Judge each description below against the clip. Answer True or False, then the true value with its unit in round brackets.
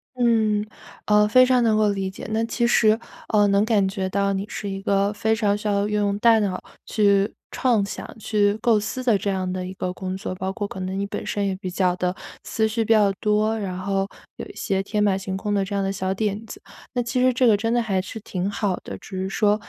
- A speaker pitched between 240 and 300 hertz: False (205 Hz)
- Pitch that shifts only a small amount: True (2.2 semitones)